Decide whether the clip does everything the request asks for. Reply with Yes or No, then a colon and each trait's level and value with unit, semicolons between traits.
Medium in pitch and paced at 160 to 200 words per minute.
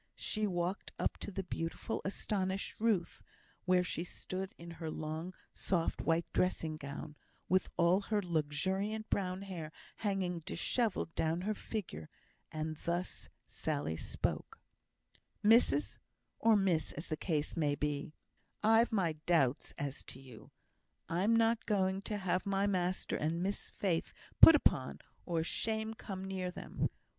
No: medium, 180 Hz; average, 140 wpm